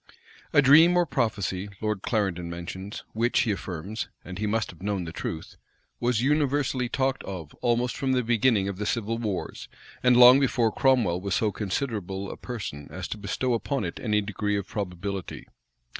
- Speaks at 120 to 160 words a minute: No, average, 175 wpm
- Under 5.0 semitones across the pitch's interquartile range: Yes, average, 4.4 semitones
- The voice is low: Yes, low, 105 Hz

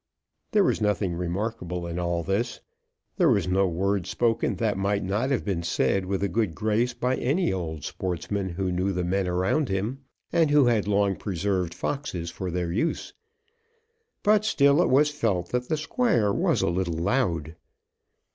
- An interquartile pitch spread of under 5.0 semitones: No, wide, 5.4 semitones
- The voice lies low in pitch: Yes, low, 100 Hz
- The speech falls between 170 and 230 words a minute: Yes, average, 175 wpm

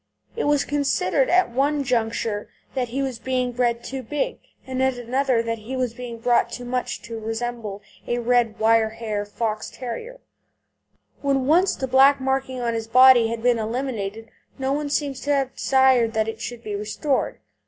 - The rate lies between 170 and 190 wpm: Yes, average, 180 wpm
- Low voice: No, high, 245 Hz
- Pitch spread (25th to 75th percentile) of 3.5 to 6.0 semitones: No, average, 2.7 semitones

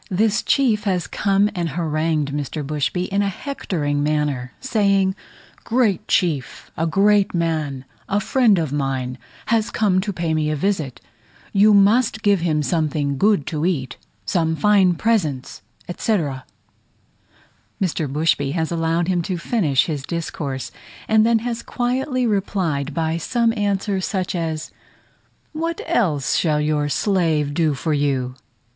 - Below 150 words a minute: Yes, average, 140 wpm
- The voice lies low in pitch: No, medium, 170 Hz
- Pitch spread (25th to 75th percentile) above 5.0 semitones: Yes, wide, 5.5 semitones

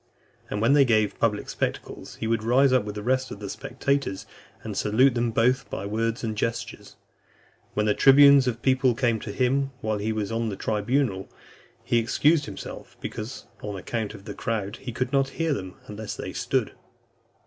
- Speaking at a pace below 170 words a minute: No, average, 190 wpm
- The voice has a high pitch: No, low, 115 Hz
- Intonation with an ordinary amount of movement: Yes, average, 3.7 semitones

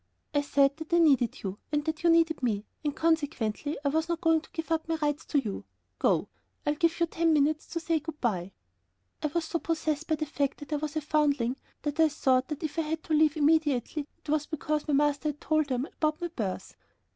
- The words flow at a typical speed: No, fast, 235 wpm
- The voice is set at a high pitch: Yes, very high, 305 Hz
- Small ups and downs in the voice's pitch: Yes, narrow, 2.1 semitones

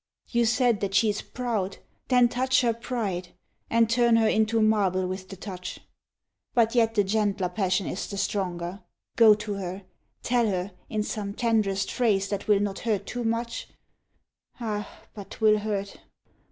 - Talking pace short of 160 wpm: No, average, 165 wpm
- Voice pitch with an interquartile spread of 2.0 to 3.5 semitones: Yes, average, 2.8 semitones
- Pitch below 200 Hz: No, high, 210 Hz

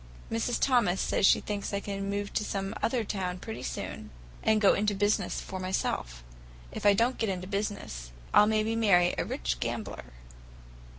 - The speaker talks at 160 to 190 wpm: Yes, average, 175 wpm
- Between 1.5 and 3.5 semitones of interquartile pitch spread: Yes, narrow, 2.5 semitones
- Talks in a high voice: Yes, high, 200 Hz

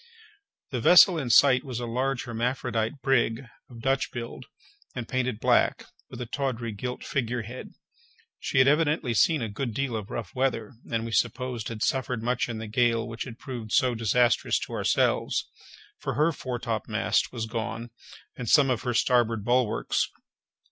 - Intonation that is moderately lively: No, narrow, 2.3 semitones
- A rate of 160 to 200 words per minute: Yes, average, 170 wpm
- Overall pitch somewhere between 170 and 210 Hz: No, low, 120 Hz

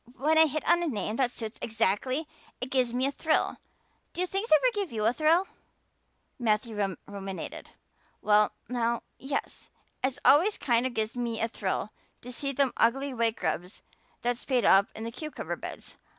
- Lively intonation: No, average, 4.5 semitones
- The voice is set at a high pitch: Yes, high, 245 Hz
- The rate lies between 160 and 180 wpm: Yes, average, 175 wpm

